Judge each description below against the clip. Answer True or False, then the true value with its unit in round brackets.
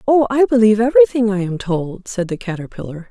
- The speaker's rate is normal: True (195 wpm)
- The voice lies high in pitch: True (215 Hz)